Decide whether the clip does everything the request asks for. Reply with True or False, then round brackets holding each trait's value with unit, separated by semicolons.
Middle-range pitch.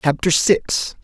True (160 Hz)